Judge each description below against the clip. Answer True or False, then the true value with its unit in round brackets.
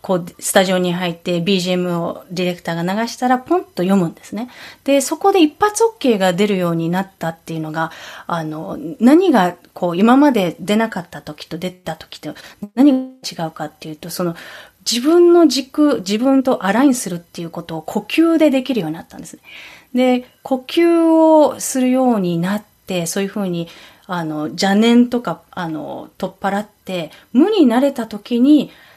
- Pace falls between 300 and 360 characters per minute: True (340 characters per minute)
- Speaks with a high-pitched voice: True (200 Hz)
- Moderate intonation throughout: False (7.0 semitones)